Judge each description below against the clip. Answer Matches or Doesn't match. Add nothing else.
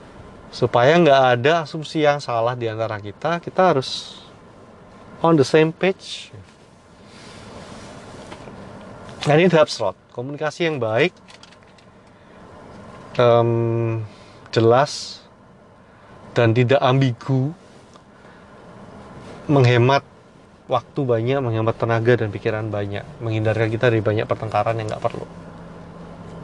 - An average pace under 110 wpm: Matches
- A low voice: Matches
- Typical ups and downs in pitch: Matches